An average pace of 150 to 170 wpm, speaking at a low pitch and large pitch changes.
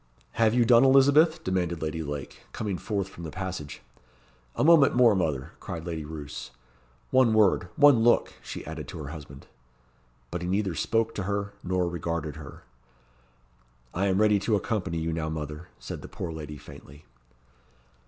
Yes: average, 165 wpm; very low, 90 Hz; wide, 5.7 semitones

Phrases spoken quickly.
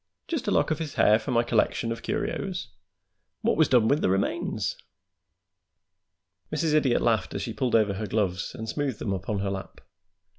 No: average, 185 wpm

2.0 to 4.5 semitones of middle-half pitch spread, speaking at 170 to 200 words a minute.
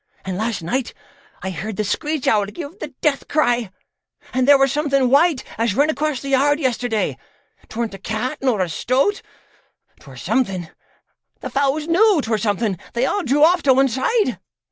No: average, 5.1 semitones; average, 175 wpm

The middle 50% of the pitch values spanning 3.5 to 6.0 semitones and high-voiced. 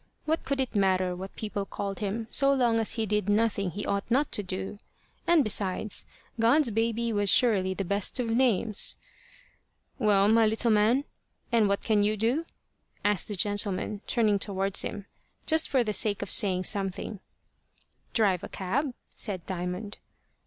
No: average, 2.7 semitones; high, 210 Hz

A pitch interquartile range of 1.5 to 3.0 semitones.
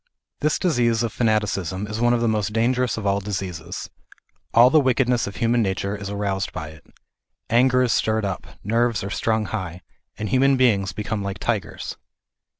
No: average, 3.4 semitones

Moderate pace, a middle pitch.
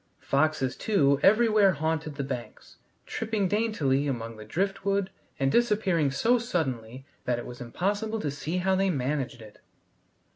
Yes: average, 145 wpm; medium, 155 Hz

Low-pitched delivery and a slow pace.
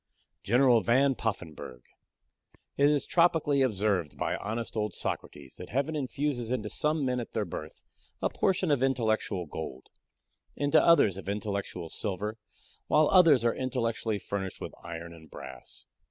No: low, 115 Hz; average, 145 wpm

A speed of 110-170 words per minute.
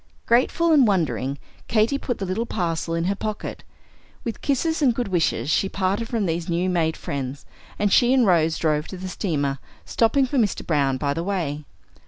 No: average, 190 wpm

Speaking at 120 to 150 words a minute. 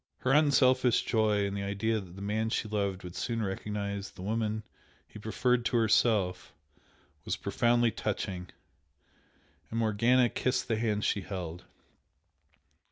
Yes: average, 140 wpm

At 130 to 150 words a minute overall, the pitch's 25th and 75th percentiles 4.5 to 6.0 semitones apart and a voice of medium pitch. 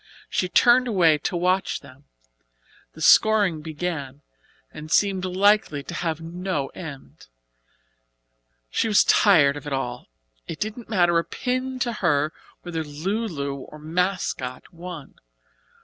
Yes: slow, 135 wpm; average, 4.8 semitones; medium, 170 Hz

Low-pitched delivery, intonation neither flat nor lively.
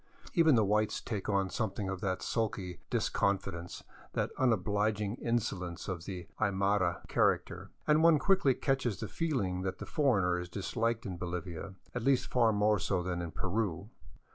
Yes: low, 100 Hz; average, 4.1 semitones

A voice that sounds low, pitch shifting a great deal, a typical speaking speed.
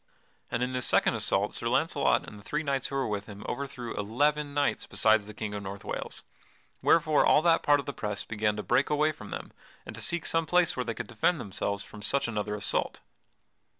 No: low, 120 Hz; wide, 5.8 semitones; fast, 220 wpm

